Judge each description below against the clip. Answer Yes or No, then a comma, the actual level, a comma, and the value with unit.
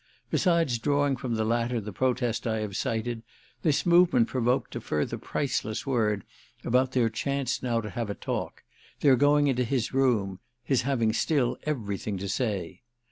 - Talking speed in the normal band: Yes, average, 165 wpm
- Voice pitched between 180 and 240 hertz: No, low, 120 Hz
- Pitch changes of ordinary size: Yes, average, 3.7 semitones